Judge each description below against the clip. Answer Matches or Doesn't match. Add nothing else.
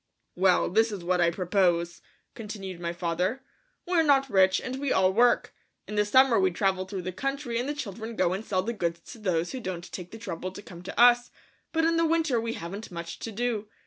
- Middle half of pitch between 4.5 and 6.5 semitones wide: Matches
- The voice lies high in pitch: Matches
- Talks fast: Matches